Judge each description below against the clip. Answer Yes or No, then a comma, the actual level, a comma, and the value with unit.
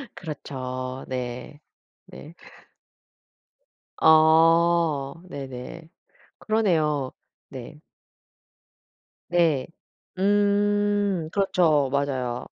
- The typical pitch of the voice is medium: Yes, medium, 155 Hz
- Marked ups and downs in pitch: No, average, 4.7 semitones